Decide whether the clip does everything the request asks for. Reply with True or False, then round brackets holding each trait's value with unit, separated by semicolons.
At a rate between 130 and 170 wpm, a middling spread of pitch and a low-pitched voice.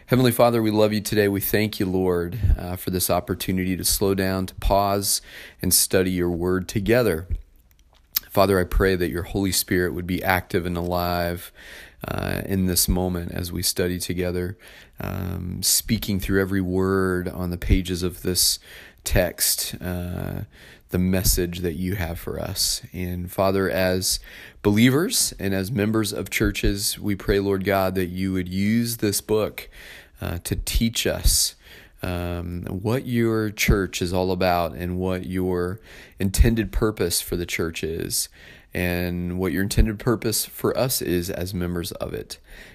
False (160 wpm; 2.1 semitones; 95 Hz)